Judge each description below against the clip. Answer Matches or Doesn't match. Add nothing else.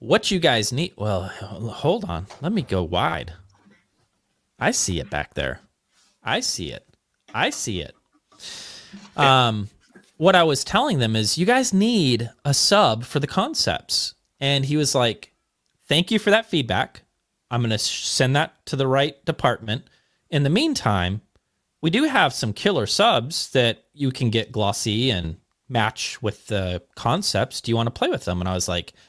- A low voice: Matches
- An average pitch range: Doesn't match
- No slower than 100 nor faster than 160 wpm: Doesn't match